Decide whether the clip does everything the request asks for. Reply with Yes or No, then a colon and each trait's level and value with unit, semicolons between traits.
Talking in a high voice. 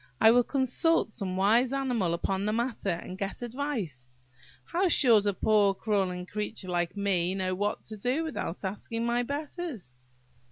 Yes: high, 210 Hz